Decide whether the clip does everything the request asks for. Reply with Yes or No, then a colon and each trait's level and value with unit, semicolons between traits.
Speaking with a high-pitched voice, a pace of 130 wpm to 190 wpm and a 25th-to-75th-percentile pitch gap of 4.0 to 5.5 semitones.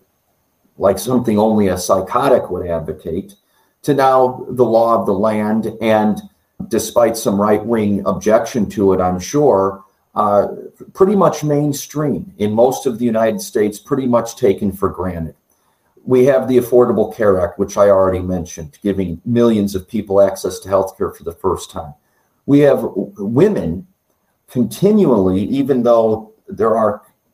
No: low, 110 Hz; average, 150 wpm; average, 4.6 semitones